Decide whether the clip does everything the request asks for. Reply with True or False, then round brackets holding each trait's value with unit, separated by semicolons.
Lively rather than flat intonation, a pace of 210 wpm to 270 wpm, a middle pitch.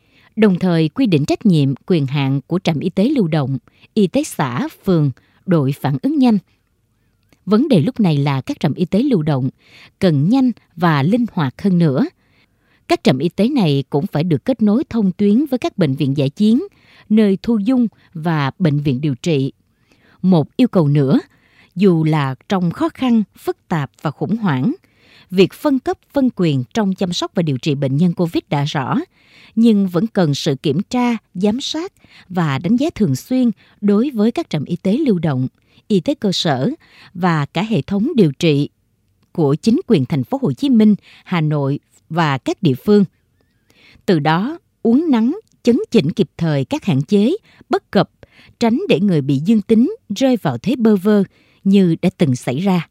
False (7.6 semitones; 195 wpm; 180 Hz)